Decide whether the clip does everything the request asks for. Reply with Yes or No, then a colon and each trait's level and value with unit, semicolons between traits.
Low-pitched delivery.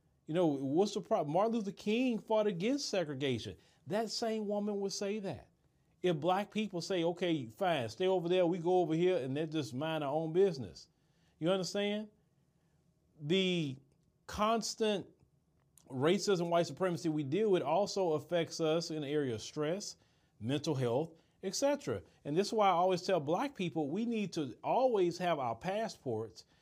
No: medium, 175 Hz